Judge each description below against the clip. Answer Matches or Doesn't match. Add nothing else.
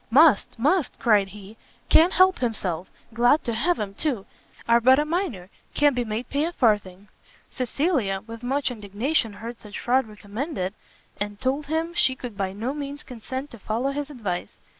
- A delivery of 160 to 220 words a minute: Matches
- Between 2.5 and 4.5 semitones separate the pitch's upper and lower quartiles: Doesn't match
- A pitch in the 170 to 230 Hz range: Doesn't match